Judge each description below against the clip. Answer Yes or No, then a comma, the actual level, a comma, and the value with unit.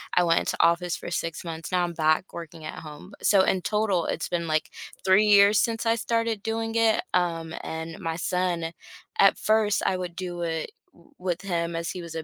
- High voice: No, medium, 180 Hz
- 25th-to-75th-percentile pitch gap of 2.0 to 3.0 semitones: No, average, 3.5 semitones